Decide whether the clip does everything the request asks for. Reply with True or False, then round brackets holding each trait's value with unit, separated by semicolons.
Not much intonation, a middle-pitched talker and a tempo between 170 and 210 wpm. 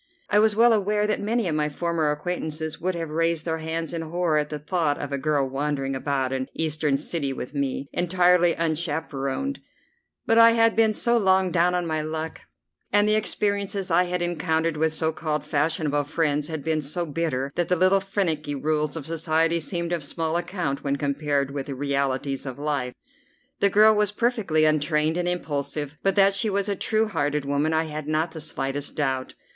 False (3.6 semitones; 160 Hz; 195 wpm)